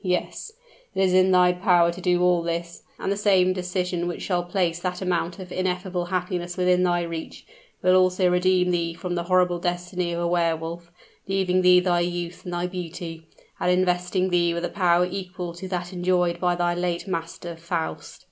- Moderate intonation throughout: No, narrow, 1.0 semitones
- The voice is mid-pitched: Yes, medium, 180 Hz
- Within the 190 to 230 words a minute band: Yes, average, 195 wpm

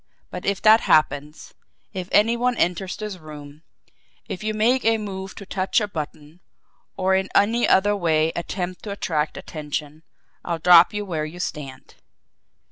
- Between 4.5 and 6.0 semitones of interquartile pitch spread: Yes, average, 4.9 semitones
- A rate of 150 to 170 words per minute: Yes, average, 160 wpm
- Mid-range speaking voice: Yes, medium, 180 Hz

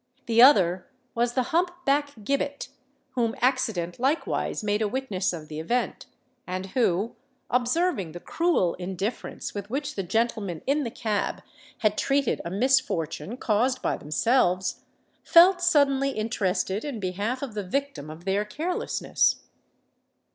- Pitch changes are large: Yes, wide, 6.3 semitones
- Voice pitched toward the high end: Yes, high, 230 Hz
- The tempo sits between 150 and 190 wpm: No, average, 140 wpm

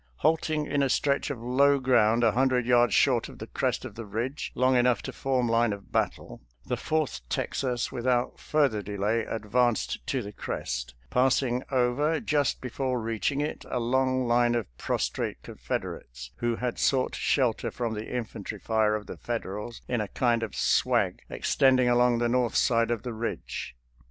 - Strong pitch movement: No, narrow, 2.5 semitones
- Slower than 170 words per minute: No, average, 175 wpm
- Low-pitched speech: Yes, low, 120 Hz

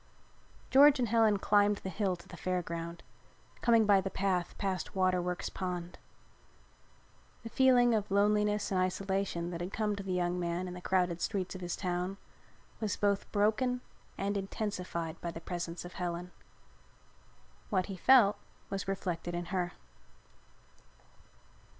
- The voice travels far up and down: No, average, 2.7 semitones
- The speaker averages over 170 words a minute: No, average, 150 wpm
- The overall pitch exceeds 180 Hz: Yes, high, 190 Hz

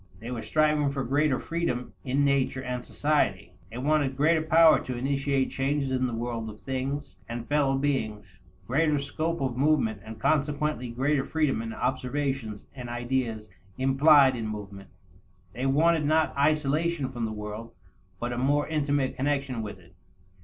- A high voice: No, low, 135 Hz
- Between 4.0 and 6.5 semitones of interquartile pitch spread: No, average, 3.5 semitones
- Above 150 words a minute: Yes, average, 160 wpm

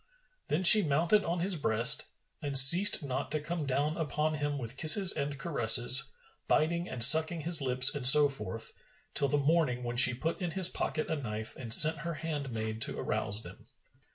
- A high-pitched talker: No, medium, 145 Hz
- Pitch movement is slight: No, average, 4.5 semitones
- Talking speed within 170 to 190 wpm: Yes, average, 185 wpm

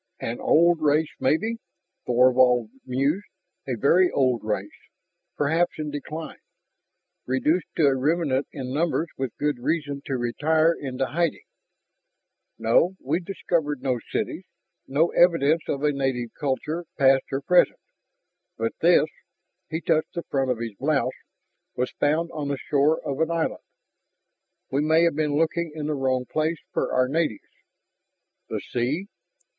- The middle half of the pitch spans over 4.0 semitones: No, average, 3.6 semitones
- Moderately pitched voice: Yes, medium, 145 Hz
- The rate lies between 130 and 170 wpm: Yes, average, 145 wpm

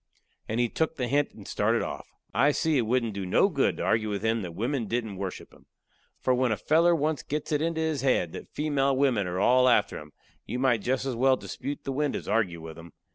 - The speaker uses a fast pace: Yes, fast, 240 wpm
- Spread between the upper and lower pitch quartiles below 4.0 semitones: No, average, 5.1 semitones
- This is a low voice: Yes, low, 125 Hz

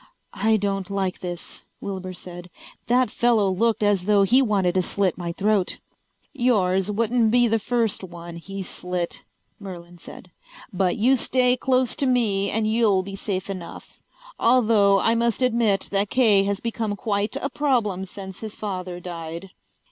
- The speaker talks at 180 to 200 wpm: No, average, 160 wpm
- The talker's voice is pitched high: Yes, high, 200 Hz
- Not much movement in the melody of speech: No, average, 3.6 semitones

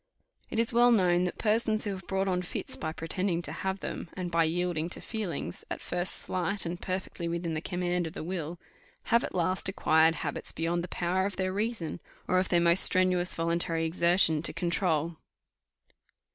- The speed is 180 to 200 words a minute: Yes, average, 185 wpm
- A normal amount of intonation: No, narrow, 2.1 semitones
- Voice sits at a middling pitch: Yes, medium, 180 Hz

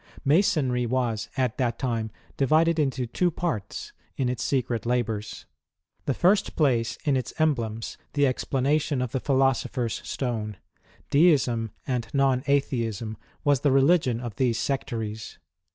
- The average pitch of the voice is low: Yes, low, 130 Hz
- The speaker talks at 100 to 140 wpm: Yes, slow, 135 wpm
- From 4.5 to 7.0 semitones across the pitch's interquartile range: No, average, 3.5 semitones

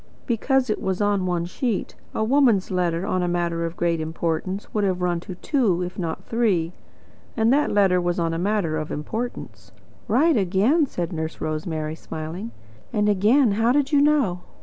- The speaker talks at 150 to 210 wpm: Yes, average, 180 wpm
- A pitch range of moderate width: Yes, average, 5.0 semitones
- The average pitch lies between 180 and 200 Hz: Yes, medium, 185 Hz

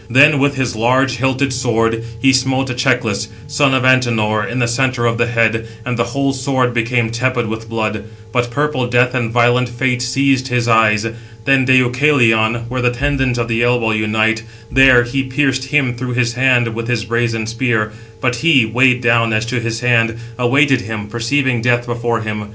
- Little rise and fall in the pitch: Yes, narrow, 2.2 semitones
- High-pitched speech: No, low, 120 Hz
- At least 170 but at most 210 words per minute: Yes, average, 185 wpm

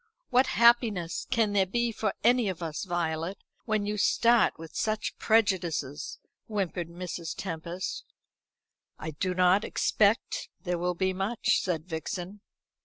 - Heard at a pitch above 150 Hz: Yes, high, 190 Hz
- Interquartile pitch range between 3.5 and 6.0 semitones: Yes, average, 4.0 semitones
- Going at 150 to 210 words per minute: No, slow, 135 wpm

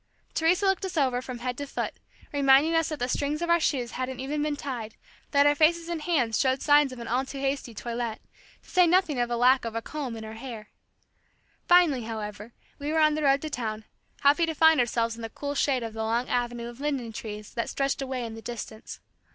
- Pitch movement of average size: Yes, average, 4.2 semitones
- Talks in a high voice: Yes, very high, 260 Hz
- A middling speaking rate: No, fast, 235 wpm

